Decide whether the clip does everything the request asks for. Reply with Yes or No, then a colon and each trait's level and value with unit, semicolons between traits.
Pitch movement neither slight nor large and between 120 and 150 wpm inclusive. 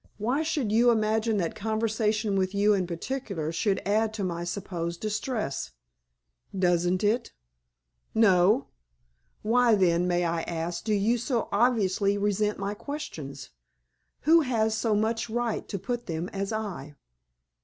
Yes: average, 4.0 semitones; average, 140 wpm